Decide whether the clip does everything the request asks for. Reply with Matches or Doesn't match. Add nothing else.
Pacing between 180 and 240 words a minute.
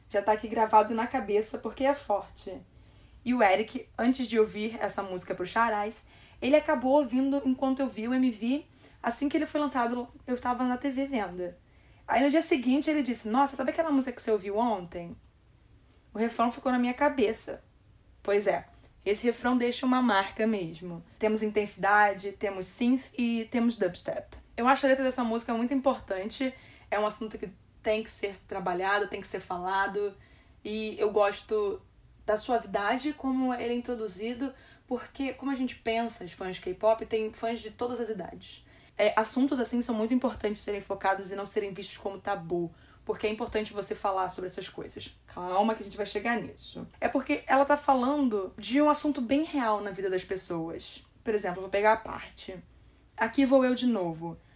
Matches